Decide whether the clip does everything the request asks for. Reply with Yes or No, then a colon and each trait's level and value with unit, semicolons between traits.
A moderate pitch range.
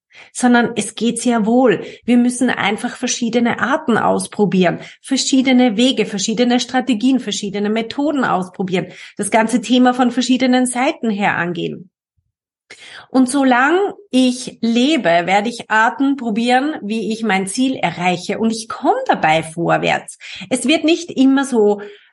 Yes: average, 3.9 semitones